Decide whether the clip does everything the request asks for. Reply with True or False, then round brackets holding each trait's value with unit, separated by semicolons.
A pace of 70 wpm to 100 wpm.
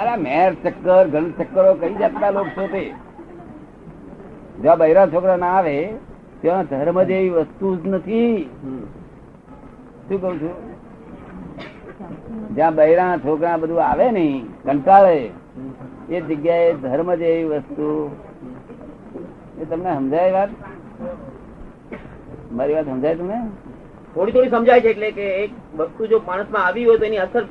True (85 wpm)